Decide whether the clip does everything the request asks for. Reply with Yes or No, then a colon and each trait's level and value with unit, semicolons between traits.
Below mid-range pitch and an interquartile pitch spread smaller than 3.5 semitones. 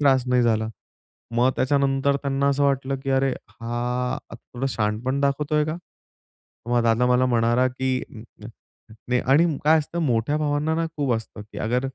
Yes: low, 130 Hz; average, 2.7 semitones